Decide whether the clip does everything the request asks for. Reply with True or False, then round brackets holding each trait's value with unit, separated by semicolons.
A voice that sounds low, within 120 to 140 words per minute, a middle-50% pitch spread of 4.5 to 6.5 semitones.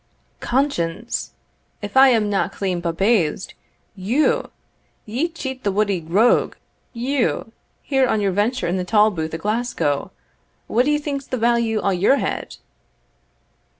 False (220 Hz; 135 wpm; 5.1 semitones)